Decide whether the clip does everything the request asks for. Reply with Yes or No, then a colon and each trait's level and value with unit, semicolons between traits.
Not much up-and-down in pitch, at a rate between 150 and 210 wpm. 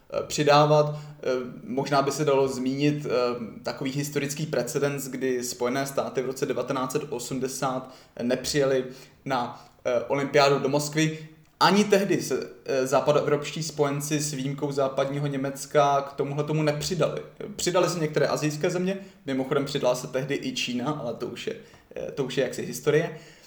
No: narrow, 2.1 semitones; average, 135 wpm